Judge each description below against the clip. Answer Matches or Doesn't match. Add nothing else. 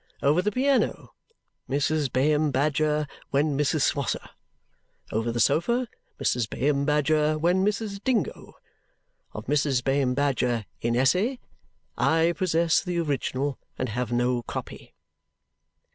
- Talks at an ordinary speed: Doesn't match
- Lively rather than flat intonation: Doesn't match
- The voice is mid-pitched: Matches